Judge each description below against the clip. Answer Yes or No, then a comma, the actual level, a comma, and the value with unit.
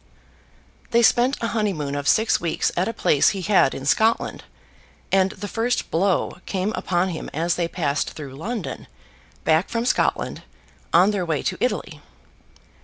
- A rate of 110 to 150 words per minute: No, average, 160 wpm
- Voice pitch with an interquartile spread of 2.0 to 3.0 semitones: No, wide, 5.4 semitones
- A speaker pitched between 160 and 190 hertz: Yes, medium, 185 Hz